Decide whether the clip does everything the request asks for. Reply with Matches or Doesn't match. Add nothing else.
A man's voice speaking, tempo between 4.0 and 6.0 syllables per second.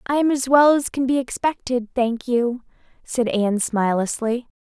Doesn't match